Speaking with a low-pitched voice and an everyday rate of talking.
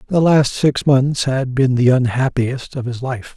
Yes: low, 130 Hz; average, 195 wpm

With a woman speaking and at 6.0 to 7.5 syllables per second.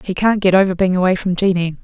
Yes: female; 6.5 syllables/s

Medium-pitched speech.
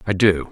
No: very low, 90 Hz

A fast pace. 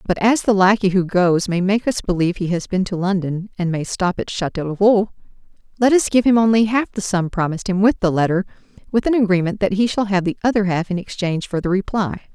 Yes: fast, 235 wpm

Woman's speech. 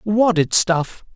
No: male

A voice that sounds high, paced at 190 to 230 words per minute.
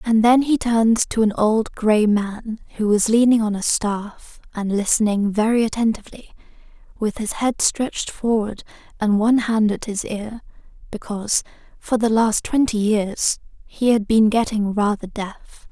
No: high, 220 Hz; average, 160 wpm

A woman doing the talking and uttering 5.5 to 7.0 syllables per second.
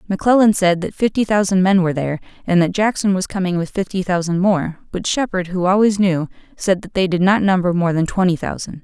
Yes: female; 6.0 syllables/s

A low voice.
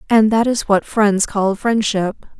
No: high, 210 Hz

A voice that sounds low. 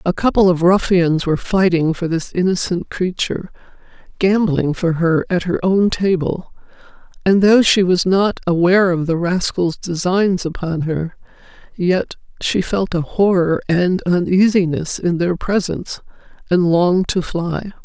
No: medium, 180 Hz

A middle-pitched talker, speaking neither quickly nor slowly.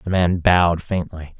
No: very low, 85 Hz; average, 170 wpm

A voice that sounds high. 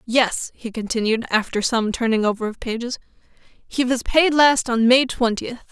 Yes: high, 235 Hz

